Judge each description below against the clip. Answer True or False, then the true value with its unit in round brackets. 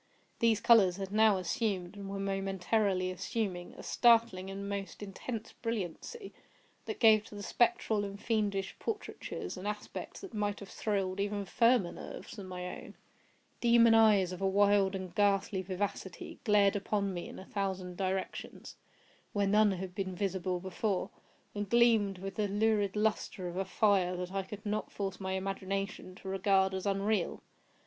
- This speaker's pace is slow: False (165 wpm)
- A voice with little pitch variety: True (1.9 semitones)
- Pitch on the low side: False (200 Hz)